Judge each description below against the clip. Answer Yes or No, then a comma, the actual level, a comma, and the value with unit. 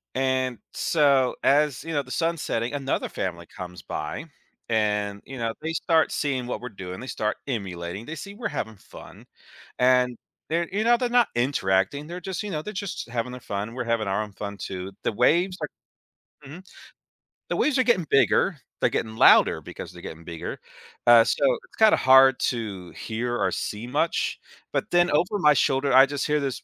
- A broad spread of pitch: Yes, wide, 6.8 semitones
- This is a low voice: Yes, low, 130 Hz